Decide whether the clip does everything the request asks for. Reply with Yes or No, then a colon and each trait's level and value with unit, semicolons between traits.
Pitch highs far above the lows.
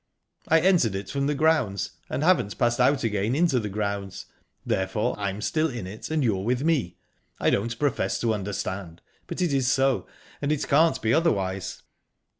Yes: wide, 6.5 semitones